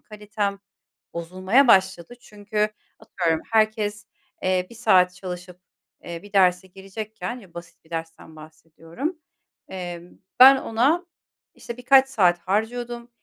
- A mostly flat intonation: No, average, 4.3 semitones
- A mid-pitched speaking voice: No, high, 195 Hz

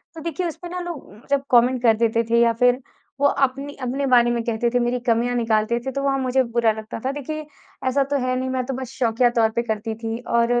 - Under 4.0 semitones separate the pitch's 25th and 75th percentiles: Yes, average, 2.7 semitones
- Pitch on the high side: Yes, high, 245 Hz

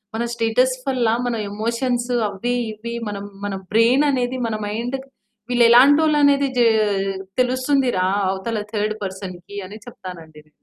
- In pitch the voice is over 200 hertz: Yes, high, 235 Hz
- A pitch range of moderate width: Yes, average, 3.7 semitones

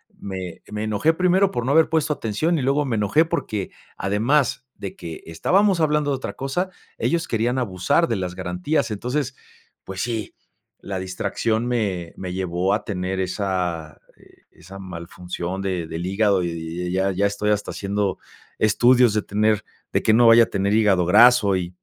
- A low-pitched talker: Yes, low, 105 Hz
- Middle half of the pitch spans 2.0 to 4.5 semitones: No, average, 5.1 semitones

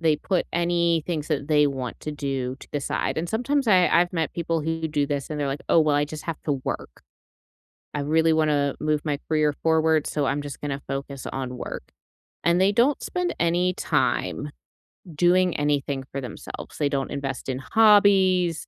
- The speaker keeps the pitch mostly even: No, average, 3.3 semitones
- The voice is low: No, medium, 155 Hz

